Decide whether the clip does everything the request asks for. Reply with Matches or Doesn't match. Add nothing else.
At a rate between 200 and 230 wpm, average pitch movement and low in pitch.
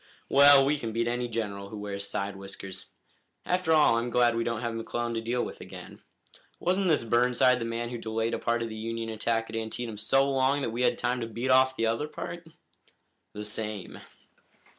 Doesn't match